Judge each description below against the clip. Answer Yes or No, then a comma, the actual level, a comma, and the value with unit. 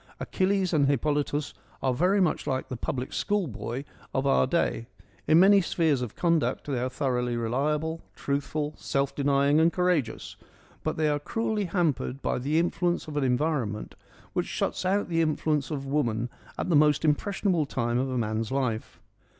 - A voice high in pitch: No, medium, 145 Hz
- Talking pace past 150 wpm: Yes, average, 170 wpm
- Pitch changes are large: No, average, 4.2 semitones